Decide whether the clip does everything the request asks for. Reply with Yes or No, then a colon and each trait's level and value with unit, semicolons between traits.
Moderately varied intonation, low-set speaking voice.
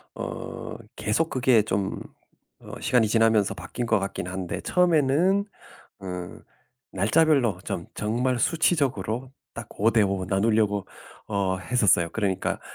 Yes: average, 4.8 semitones; low, 110 Hz